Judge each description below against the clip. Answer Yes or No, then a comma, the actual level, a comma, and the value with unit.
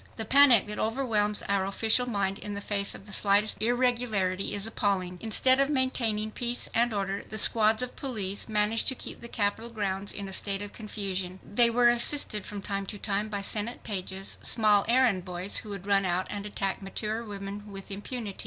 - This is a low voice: No, high, 210 Hz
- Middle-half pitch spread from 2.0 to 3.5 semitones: Yes, average, 2.7 semitones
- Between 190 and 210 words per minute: Yes, average, 195 wpm